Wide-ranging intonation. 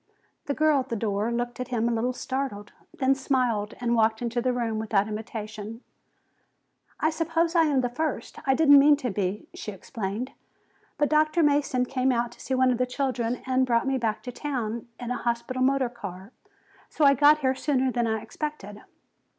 No: average, 3.3 semitones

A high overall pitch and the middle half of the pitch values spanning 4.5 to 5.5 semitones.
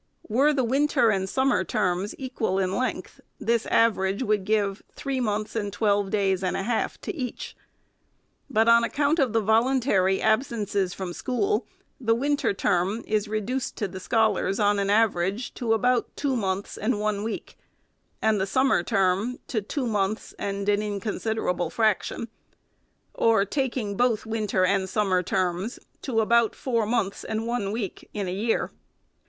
No: high, 215 Hz; average, 3.1 semitones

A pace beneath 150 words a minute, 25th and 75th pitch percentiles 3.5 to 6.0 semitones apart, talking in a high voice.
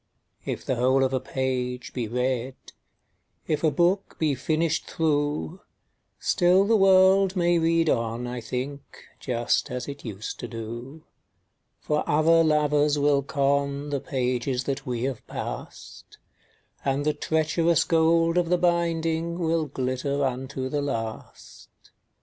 No: average, 140 wpm; average, 4.3 semitones; medium, 145 Hz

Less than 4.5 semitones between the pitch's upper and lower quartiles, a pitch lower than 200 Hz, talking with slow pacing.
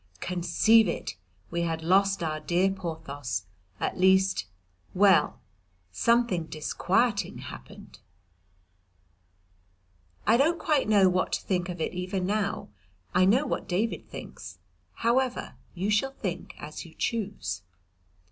Yes: average, 4.0 semitones; high, 190 Hz; slow, 120 wpm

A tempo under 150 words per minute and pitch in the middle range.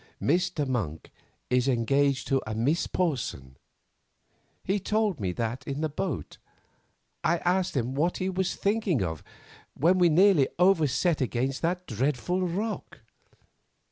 Yes: average, 140 wpm; medium, 150 Hz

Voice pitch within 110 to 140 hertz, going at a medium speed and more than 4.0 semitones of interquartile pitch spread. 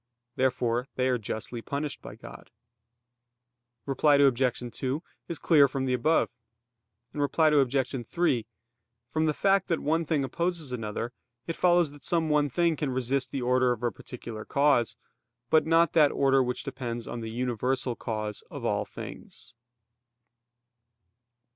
No: low, 135 Hz; average, 150 wpm; average, 3.7 semitones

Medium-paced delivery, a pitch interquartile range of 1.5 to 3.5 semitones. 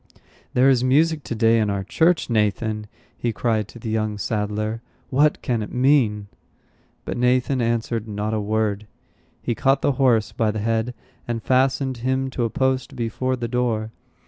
Yes: average, 170 wpm; average, 3.1 semitones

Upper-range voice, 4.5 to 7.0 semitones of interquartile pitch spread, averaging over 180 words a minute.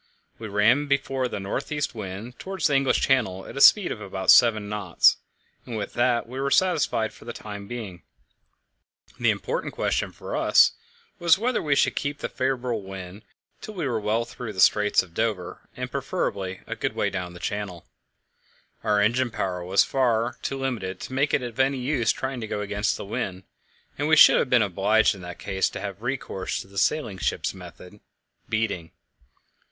No: low, 110 Hz; average, 5.2 semitones; average, 190 wpm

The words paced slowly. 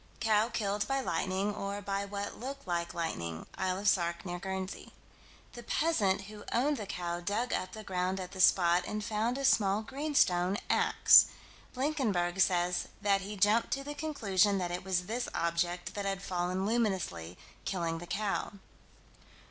No: average, 165 wpm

